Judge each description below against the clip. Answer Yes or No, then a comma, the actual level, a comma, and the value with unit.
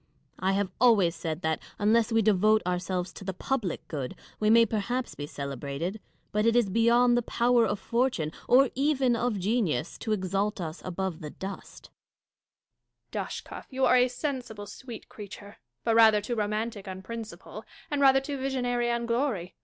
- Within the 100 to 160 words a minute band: No, average, 170 wpm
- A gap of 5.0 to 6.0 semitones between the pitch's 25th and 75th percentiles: No, average, 4.3 semitones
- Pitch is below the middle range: No, high, 215 Hz